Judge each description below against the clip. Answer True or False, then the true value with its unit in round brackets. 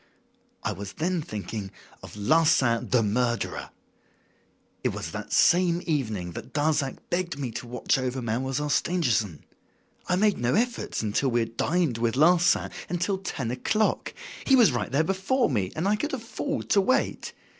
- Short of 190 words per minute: True (165 wpm)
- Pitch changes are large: True (7.5 semitones)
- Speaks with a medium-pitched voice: True (145 Hz)